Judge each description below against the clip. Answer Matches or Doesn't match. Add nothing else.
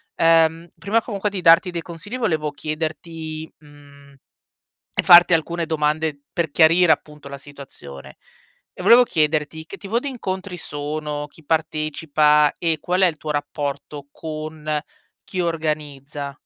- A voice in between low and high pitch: Matches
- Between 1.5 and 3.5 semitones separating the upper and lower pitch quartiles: Matches